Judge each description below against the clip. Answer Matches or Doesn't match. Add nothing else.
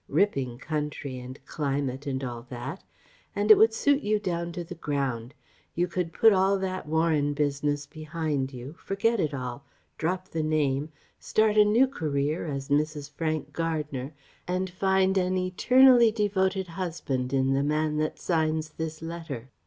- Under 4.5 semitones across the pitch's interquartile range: Doesn't match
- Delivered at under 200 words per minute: Matches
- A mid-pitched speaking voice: Matches